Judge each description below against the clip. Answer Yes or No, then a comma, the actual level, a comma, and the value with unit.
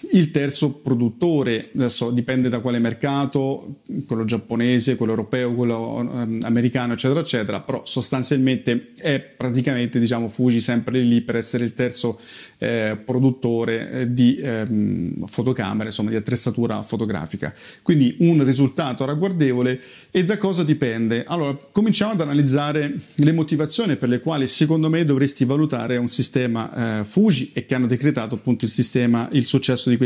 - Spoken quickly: No, average, 145 wpm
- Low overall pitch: Yes, low, 125 Hz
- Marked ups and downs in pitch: No, average, 3.1 semitones